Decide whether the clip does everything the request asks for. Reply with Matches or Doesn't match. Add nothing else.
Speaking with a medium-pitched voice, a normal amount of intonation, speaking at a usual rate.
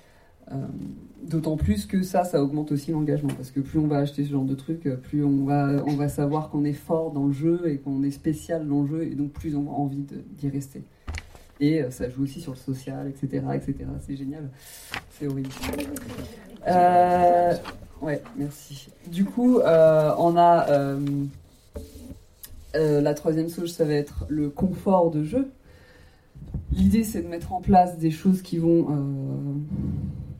Matches